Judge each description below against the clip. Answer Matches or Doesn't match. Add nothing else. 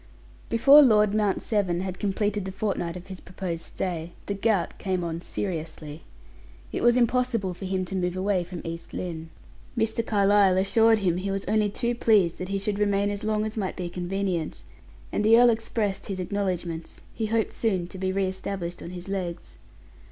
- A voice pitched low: Doesn't match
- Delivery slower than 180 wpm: Doesn't match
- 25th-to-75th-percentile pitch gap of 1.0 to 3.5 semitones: Matches